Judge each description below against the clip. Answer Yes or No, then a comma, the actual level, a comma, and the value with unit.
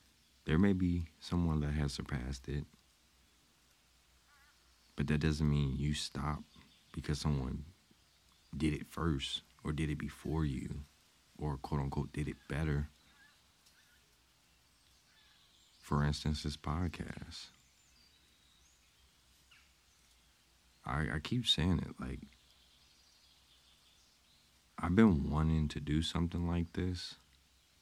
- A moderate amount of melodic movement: No, narrow, 2.1 semitones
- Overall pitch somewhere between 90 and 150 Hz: No, very low, 75 Hz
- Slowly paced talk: Yes, slow, 105 wpm